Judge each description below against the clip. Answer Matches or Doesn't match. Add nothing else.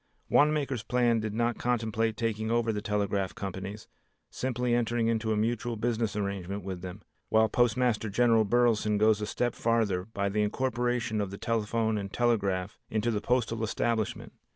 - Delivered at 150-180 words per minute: Matches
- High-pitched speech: Doesn't match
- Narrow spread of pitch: Matches